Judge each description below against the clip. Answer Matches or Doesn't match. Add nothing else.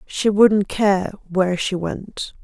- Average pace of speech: Matches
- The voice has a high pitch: Matches